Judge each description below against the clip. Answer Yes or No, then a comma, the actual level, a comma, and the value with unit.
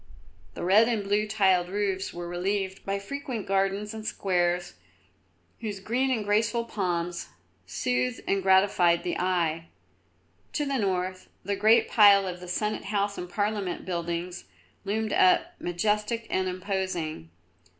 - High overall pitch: Yes, high, 195 Hz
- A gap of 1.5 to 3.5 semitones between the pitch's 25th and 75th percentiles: Yes, average, 2.9 semitones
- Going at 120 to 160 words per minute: Yes, average, 140 wpm